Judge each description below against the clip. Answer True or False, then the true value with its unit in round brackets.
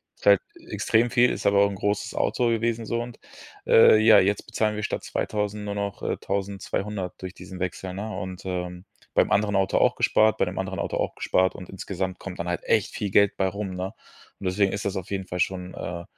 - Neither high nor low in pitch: False (100 Hz)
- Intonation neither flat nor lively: False (2.1 semitones)